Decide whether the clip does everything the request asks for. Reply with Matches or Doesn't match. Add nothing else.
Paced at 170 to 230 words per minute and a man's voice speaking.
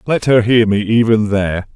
Matches